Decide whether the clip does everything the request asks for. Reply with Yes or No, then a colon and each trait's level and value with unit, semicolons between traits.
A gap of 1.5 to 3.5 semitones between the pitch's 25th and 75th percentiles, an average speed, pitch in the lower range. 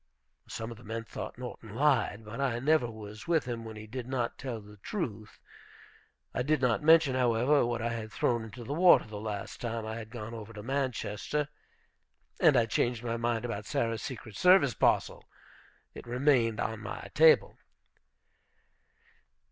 Yes: average, 3.0 semitones; average, 170 wpm; low, 115 Hz